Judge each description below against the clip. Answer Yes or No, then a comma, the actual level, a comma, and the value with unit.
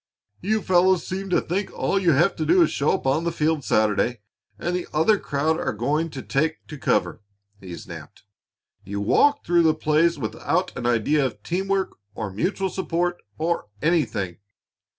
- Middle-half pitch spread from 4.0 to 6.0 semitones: Yes, average, 5.2 semitones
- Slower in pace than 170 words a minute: No, average, 185 wpm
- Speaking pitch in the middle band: Yes, medium, 160 Hz